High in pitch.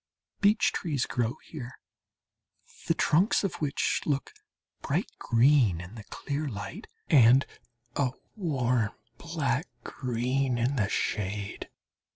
No: low, 130 Hz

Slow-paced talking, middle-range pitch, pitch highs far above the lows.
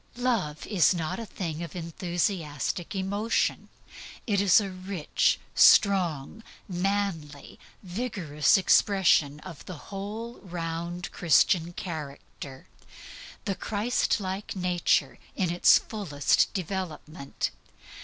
No: slow, 95 wpm; medium, 180 Hz; average, 3.6 semitones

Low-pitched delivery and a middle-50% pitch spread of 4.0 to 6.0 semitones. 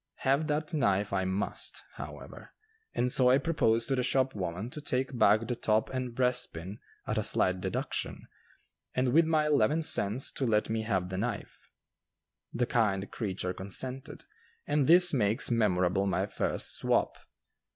Yes: low, 120 Hz; average, 5.0 semitones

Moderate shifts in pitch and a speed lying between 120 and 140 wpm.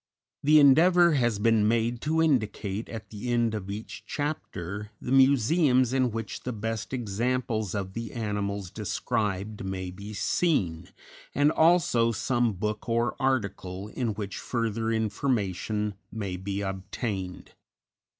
Yes: average, 4.0 semitones; slow, 135 wpm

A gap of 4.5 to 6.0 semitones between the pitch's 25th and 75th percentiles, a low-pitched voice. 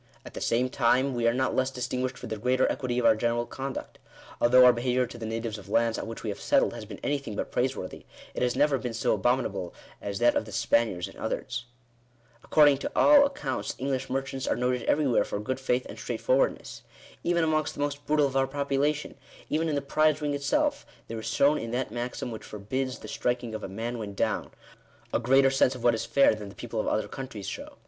No: average, 3.2 semitones; low, 125 Hz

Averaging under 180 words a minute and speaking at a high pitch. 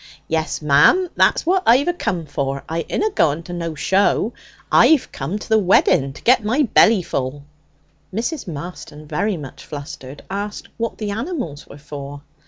No: average, 165 wpm; medium, 175 Hz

